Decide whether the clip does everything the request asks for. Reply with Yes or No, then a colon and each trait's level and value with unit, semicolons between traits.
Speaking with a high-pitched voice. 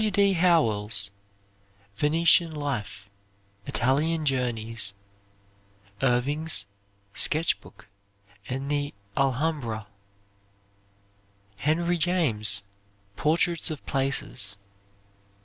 No: medium, 140 Hz